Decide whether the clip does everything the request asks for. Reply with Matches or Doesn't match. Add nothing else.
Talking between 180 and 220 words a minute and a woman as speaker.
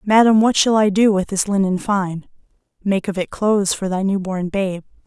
Matches